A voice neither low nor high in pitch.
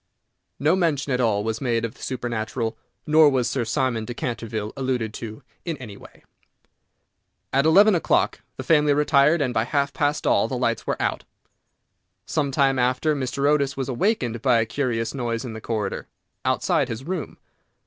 No: low, 130 Hz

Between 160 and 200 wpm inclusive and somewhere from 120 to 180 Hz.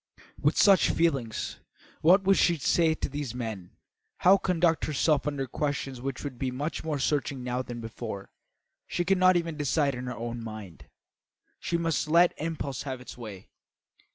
Yes: average, 170 wpm; medium, 140 Hz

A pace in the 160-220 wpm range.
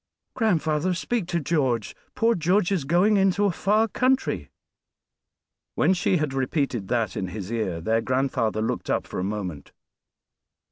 No: average, 150 wpm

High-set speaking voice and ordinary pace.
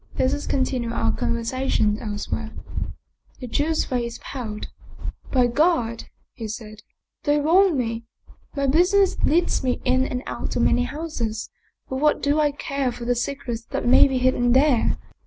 Yes: very high, 255 Hz; average, 175 wpm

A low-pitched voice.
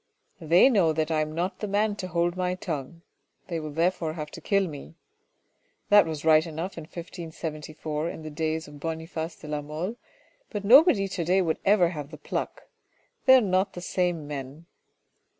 No: medium, 165 Hz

